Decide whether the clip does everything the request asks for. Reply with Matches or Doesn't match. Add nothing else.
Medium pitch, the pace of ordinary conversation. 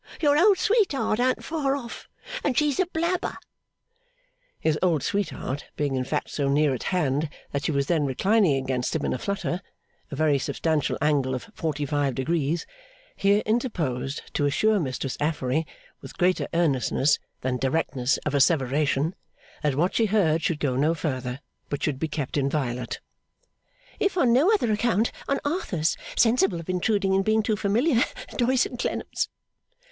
Matches